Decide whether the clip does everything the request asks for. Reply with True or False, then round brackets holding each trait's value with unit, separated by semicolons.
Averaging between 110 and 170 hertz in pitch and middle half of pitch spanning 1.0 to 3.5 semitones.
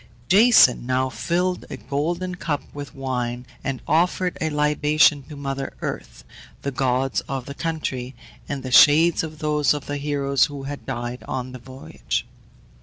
True (140 Hz; 2.9 semitones)